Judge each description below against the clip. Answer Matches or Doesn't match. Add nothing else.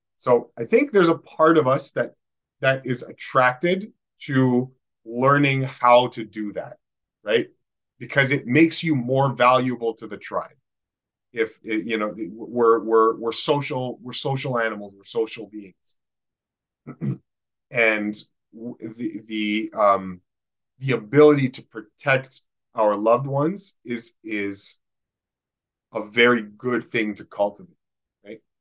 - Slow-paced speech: Matches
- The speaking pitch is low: Matches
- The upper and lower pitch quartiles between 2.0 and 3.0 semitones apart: Doesn't match